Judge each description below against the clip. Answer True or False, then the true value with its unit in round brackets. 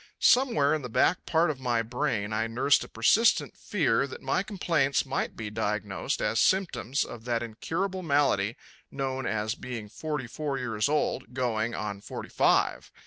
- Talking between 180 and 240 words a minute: False (165 wpm)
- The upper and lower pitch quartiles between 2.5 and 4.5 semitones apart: False (5.2 semitones)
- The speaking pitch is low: True (130 Hz)